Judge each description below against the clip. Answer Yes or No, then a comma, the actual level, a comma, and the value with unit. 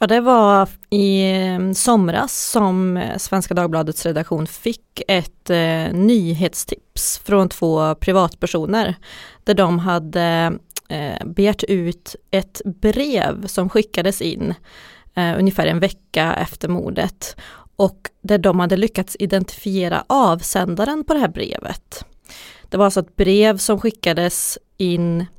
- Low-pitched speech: No, high, 190 Hz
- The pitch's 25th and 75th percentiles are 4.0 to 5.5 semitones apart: No, average, 2.8 semitones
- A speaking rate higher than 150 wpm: No, slow, 125 wpm